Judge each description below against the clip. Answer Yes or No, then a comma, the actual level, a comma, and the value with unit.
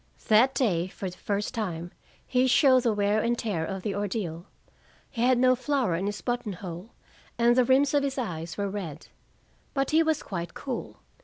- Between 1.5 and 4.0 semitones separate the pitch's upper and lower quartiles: No, wide, 5.5 semitones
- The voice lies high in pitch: Yes, high, 215 Hz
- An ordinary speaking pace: Yes, average, 190 wpm